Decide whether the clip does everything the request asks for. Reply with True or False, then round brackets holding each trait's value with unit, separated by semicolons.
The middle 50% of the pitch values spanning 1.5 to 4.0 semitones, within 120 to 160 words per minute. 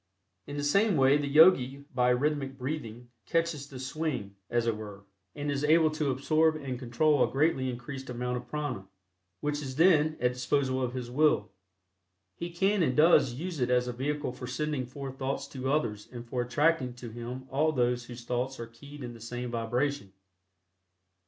False (3.4 semitones; 190 wpm)